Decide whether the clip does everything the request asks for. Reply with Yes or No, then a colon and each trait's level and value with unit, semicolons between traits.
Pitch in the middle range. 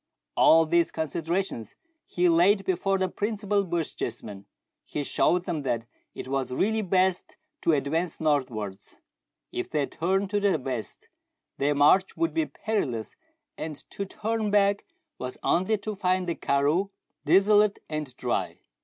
Yes: medium, 175 Hz